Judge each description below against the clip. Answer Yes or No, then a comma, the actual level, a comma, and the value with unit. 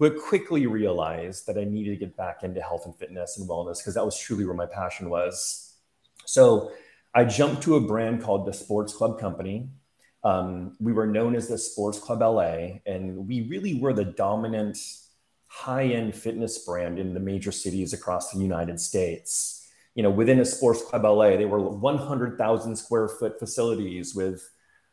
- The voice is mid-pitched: No, low, 105 Hz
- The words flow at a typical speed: Yes, average, 180 wpm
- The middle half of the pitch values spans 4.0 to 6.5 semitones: No, average, 3.4 semitones